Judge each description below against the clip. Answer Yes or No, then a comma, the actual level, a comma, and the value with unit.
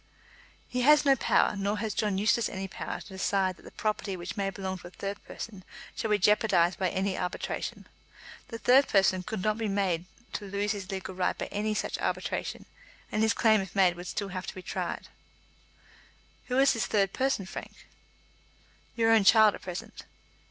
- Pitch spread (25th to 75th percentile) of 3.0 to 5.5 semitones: No, narrow, 2.5 semitones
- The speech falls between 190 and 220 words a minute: Yes, average, 195 wpm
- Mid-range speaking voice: No, high, 200 Hz